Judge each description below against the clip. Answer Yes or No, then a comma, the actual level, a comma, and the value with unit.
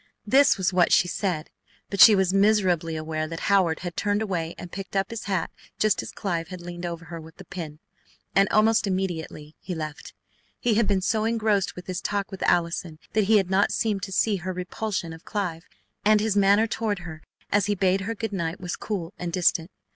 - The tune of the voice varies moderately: Yes, average, 3.2 semitones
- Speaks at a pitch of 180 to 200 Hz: Yes, high, 190 Hz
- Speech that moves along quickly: Yes, fast, 215 wpm